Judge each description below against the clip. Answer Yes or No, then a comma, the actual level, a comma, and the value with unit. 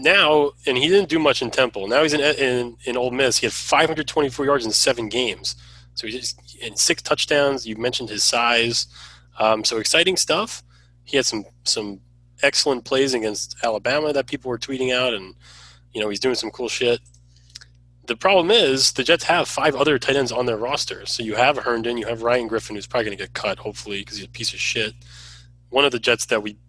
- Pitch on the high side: No, low, 115 Hz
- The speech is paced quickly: Yes, fast, 220 wpm